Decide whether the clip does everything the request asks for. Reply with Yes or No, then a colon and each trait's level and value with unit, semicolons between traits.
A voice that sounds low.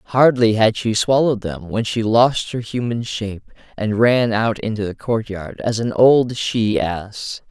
Yes: low, 110 Hz